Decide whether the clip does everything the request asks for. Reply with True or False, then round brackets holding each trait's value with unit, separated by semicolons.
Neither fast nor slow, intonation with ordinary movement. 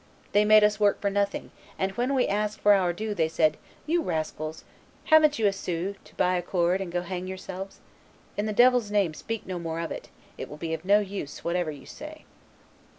False (215 wpm; 3.4 semitones)